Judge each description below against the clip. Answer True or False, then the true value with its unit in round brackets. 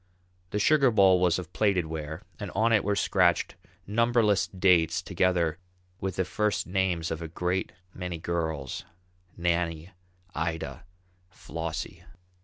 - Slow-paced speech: True (130 wpm)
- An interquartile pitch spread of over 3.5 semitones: False (3.0 semitones)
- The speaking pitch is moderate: False (90 Hz)